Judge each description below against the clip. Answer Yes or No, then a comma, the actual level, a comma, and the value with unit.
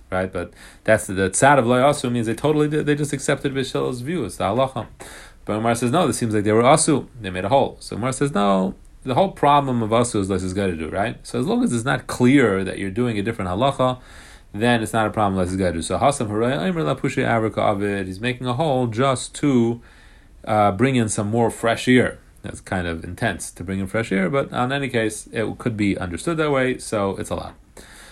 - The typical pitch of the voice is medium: No, low, 115 Hz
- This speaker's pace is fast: Yes, fast, 245 wpm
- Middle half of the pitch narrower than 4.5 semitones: No, wide, 5.4 semitones